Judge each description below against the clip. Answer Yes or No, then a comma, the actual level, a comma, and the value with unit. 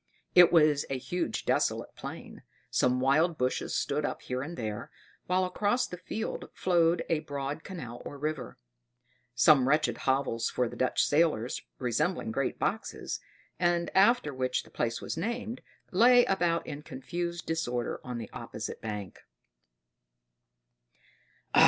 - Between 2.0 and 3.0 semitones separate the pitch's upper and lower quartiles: No, wide, 5.5 semitones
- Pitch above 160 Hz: No, medium, 150 Hz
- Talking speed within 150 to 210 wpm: No, average, 140 wpm